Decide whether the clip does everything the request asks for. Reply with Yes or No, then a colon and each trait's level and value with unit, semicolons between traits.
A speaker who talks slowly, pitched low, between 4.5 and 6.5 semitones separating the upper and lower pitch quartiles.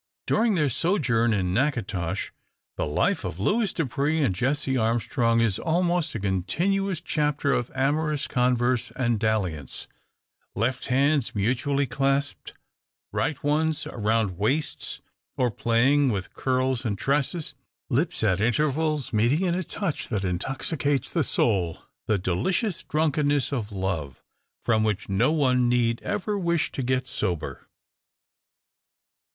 Yes: slow, 130 wpm; low, 130 Hz; wide, 5.6 semitones